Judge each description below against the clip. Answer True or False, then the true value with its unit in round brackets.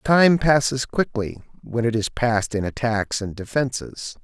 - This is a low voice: True (120 Hz)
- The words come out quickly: False (155 wpm)